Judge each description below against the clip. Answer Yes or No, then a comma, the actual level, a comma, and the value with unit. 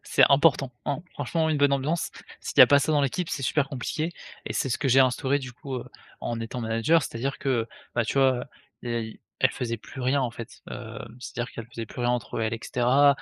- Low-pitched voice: Yes, low, 130 Hz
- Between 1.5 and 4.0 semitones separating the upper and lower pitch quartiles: Yes, average, 3.2 semitones